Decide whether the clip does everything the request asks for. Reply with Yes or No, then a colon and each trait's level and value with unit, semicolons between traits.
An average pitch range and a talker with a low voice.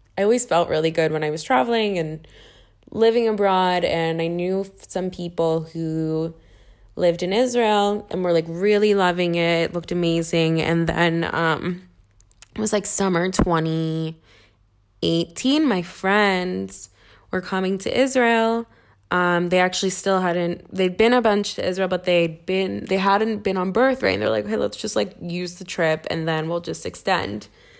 No: average, 3.3 semitones; medium, 175 Hz